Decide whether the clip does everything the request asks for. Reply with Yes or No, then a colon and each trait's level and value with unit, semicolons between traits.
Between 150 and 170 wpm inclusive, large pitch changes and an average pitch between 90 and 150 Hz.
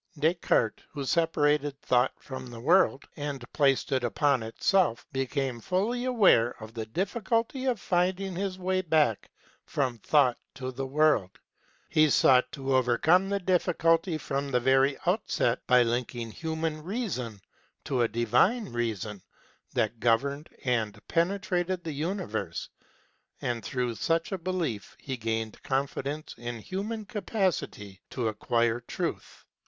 No: slow, 135 wpm; wide, 6.9 semitones; medium, 140 Hz